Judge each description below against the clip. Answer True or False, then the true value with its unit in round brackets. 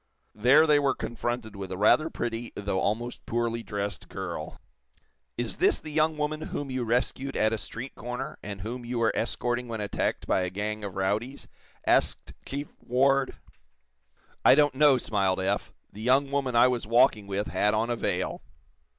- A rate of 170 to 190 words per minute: True (175 wpm)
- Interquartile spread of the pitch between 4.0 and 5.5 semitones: True (4.3 semitones)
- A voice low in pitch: True (120 Hz)